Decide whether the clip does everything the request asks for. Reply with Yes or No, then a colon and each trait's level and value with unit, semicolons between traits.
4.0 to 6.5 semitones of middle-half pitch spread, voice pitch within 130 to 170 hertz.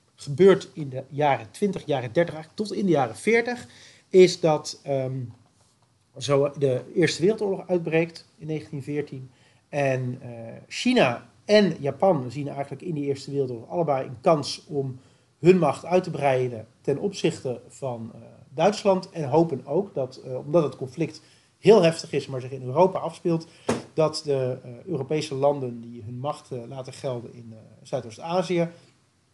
Yes: average, 4.7 semitones; medium, 140 Hz